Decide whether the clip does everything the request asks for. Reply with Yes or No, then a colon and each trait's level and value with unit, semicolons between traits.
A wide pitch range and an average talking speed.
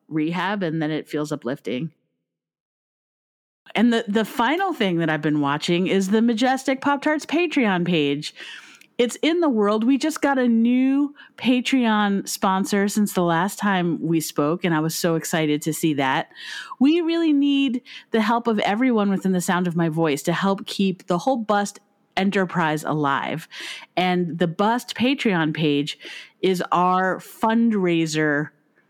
Yes: wide, 6.7 semitones; average, 160 wpm